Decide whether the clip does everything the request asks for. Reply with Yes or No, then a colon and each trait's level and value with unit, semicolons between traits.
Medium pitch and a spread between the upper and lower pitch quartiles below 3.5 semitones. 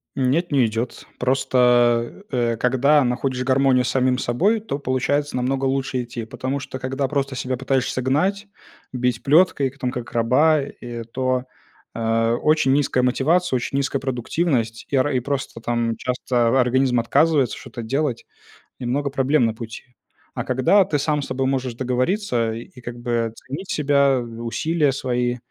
No: low, 130 Hz; narrow, 2.4 semitones